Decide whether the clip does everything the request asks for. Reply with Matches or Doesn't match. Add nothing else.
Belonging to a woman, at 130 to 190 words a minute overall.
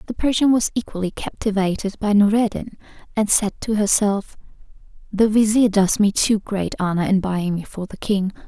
Matches